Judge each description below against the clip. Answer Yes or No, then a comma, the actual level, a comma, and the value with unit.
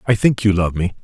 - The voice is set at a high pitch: No, low, 100 Hz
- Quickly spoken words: Yes, fast, 290 wpm